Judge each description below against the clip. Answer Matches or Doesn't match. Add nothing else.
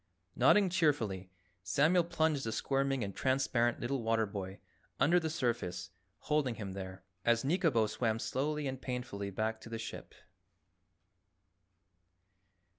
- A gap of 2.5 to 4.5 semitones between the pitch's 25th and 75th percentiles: Doesn't match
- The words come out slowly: Matches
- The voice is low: Matches